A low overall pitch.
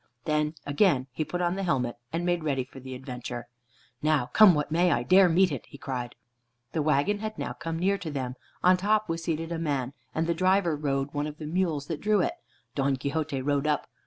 No: medium, 155 Hz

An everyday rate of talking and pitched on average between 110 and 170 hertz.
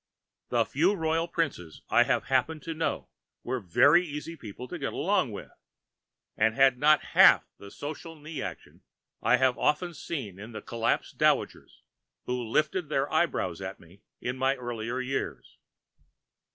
Yes: average, 160 wpm; low, 135 Hz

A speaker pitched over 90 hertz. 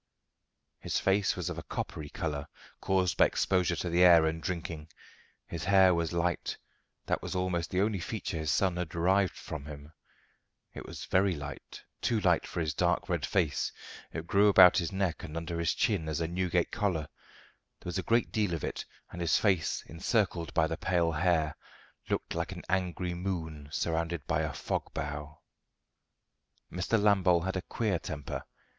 No: very low, 85 Hz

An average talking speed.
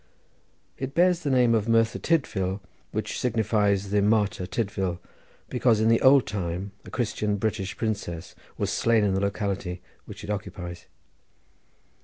Yes: average, 145 wpm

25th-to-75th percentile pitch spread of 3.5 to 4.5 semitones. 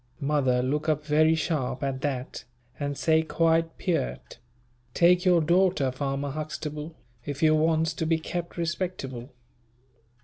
No: average, 2.9 semitones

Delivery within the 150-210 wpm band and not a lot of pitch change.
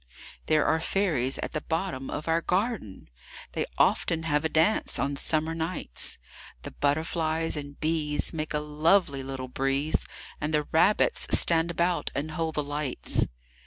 Yes: average, 155 wpm; narrow, 2.2 semitones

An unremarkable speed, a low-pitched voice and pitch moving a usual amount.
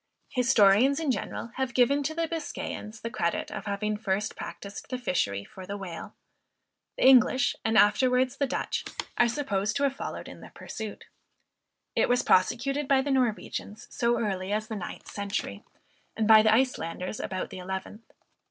No: average, 170 wpm; high, 220 Hz; average, 4.5 semitones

